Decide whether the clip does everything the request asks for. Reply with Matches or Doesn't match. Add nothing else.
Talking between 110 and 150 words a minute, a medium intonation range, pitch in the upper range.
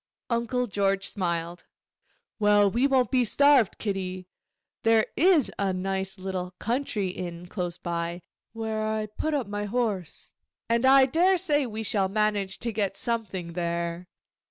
Matches